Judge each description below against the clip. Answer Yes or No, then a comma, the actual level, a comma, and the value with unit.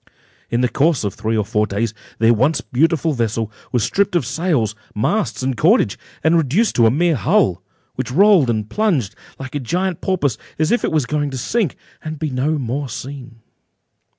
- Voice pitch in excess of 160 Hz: No, medium, 140 Hz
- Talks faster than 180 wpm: Yes, average, 190 wpm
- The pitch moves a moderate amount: No, wide, 6.0 semitones